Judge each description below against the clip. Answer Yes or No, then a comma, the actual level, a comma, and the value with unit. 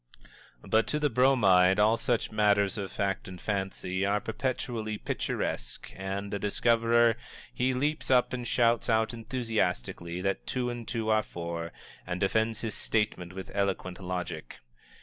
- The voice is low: Yes, low, 105 Hz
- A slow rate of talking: No, average, 150 wpm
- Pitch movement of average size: Yes, average, 3.5 semitones